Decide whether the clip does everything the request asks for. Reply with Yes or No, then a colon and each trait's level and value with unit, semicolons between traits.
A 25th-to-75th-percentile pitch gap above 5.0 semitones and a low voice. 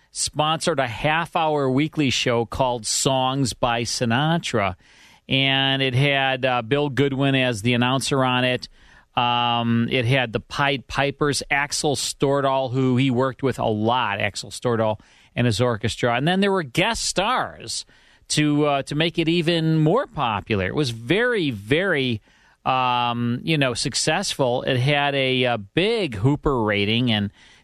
No: average, 3.3 semitones; low, 130 Hz